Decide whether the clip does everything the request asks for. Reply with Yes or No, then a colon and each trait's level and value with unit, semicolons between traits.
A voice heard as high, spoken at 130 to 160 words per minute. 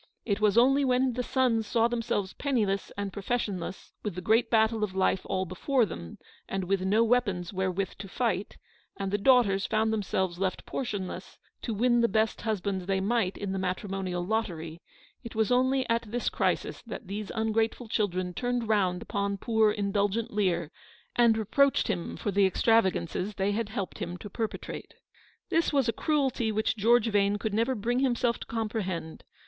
No: high, 210 Hz; average, 175 wpm